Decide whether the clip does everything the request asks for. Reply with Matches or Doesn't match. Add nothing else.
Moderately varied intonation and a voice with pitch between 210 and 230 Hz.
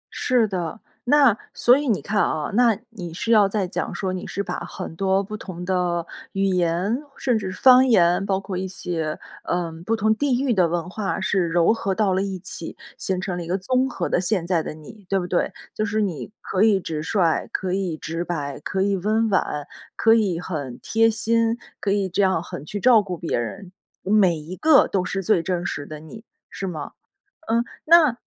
Doesn't match